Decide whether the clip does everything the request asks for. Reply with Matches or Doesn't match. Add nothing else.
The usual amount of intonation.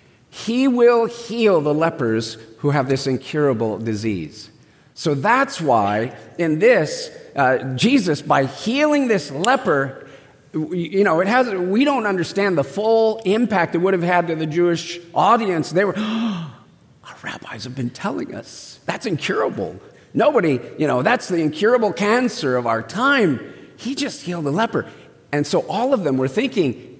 Doesn't match